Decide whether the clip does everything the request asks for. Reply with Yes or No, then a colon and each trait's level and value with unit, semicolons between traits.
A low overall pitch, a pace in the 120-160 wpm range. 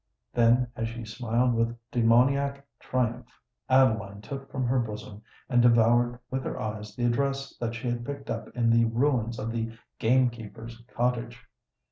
Yes: low, 120 Hz; average, 155 wpm